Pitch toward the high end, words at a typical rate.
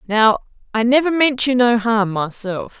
Yes: high, 235 Hz; average, 170 wpm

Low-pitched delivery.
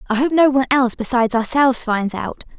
No: very high, 250 Hz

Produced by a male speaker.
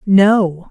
No: female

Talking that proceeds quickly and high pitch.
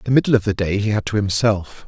No: fast, 290 wpm; low, 105 Hz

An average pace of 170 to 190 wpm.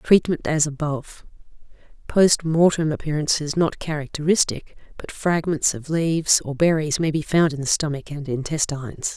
No: average, 145 wpm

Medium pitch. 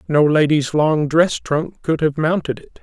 Yes: medium, 155 Hz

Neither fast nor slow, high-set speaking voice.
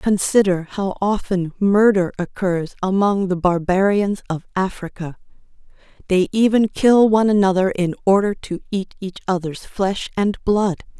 No: slow, 130 wpm; high, 195 Hz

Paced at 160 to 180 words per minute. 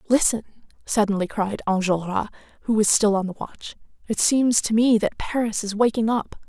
Yes: average, 175 wpm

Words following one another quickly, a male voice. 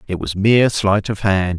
Yes: fast, 230 wpm; male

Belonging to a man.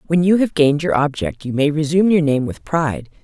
No: female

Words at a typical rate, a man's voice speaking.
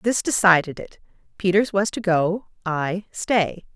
No: average, 145 wpm; female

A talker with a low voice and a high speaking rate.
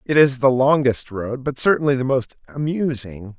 No: low, 130 Hz; average, 175 wpm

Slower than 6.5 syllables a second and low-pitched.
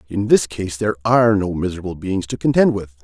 Yes: 6.2 syllables/s; low, 100 Hz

